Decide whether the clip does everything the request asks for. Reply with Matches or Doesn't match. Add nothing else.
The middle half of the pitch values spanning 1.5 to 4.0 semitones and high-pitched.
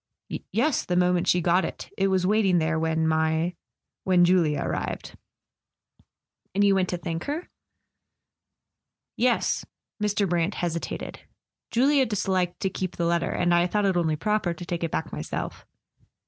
Doesn't match